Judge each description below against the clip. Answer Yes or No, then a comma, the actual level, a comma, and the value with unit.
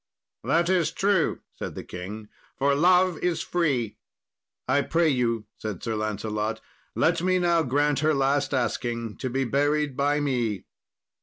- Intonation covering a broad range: Yes, wide, 5.9 semitones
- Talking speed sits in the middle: Yes, average, 150 wpm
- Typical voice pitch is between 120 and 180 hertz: Yes, medium, 140 Hz